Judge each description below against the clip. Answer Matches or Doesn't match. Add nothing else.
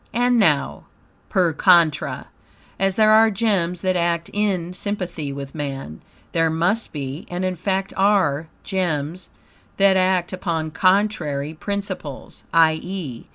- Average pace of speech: Doesn't match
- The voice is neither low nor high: Matches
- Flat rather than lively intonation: Doesn't match